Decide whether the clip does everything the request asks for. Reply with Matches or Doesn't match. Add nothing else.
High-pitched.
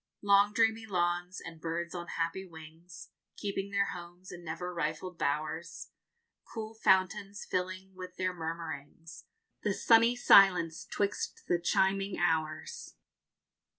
Doesn't match